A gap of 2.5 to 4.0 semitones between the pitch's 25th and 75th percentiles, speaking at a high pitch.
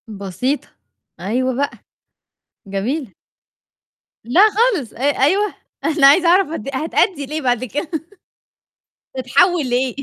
No: average, 5.2 semitones; very high, 275 Hz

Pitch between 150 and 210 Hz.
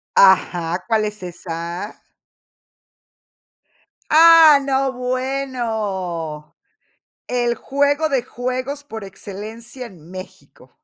No: high, 230 Hz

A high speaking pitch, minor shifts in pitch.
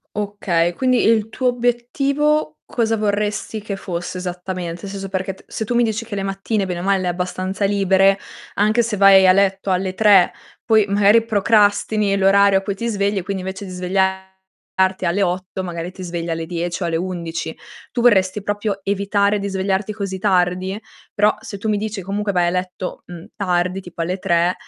Yes: high, 195 Hz; narrow, 2.2 semitones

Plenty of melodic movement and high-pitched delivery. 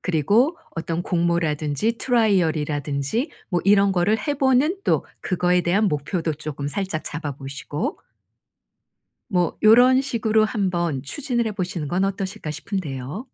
No: wide, 6.0 semitones; medium, 180 Hz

